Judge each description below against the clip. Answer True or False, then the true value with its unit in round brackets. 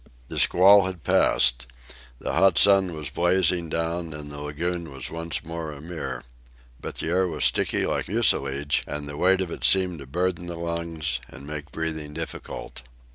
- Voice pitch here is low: True (80 Hz)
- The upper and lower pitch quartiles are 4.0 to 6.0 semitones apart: False (3.1 semitones)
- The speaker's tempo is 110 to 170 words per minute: False (180 wpm)